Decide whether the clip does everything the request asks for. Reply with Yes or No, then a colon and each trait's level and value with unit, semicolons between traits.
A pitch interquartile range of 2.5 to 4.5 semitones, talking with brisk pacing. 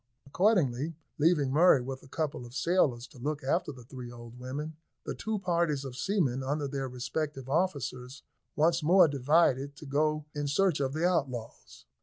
No: average, 3.8 semitones; average, 170 wpm